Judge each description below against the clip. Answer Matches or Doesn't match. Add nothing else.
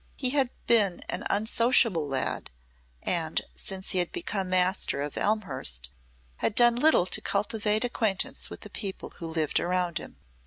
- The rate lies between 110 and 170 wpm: Matches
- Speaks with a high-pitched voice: Matches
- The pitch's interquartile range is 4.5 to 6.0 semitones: Matches